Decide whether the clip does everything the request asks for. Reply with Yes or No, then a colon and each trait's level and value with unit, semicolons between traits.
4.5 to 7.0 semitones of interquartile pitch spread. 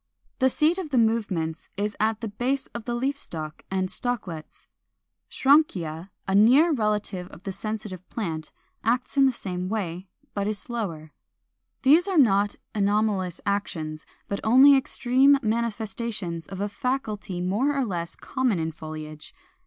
Yes: wide, 5.4 semitones